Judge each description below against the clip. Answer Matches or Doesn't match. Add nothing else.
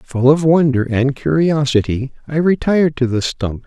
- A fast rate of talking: Doesn't match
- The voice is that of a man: Matches